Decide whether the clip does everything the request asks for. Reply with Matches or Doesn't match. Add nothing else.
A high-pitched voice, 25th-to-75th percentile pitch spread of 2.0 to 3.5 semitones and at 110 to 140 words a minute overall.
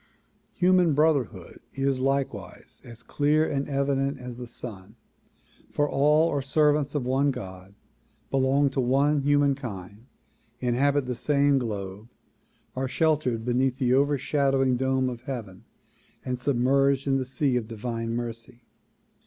Doesn't match